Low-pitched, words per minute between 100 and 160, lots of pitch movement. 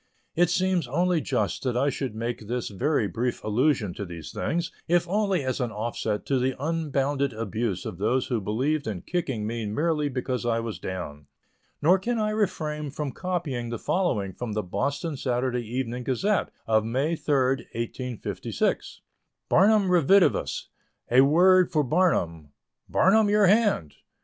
Yes: low, 130 Hz; average, 155 wpm; wide, 6.8 semitones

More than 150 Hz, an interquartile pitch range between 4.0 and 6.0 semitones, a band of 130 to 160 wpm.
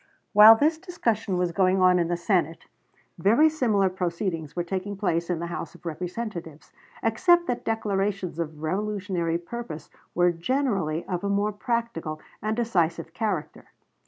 Yes: high, 190 Hz; average, 4.5 semitones; average, 150 wpm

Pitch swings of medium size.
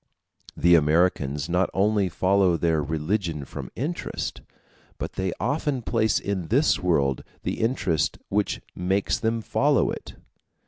Yes: average, 4.8 semitones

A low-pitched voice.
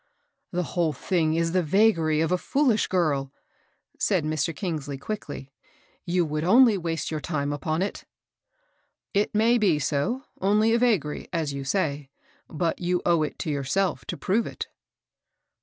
No: medium, 170 Hz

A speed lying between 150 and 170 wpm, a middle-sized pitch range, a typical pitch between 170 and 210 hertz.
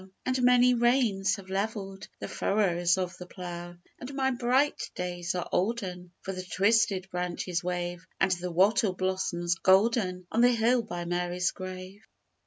Yes: average, 155 wpm; average, 4.0 semitones; high, 190 Hz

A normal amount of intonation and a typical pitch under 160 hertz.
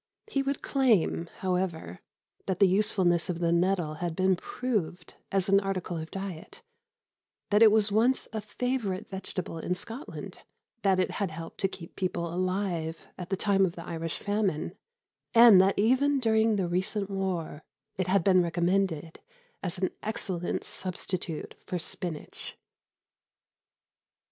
No: average, 3.1 semitones; medium, 185 Hz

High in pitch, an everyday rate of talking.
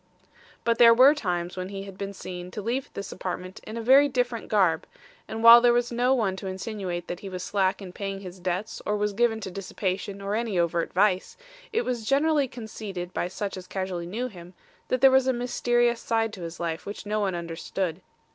No: high, 200 Hz; fast, 215 wpm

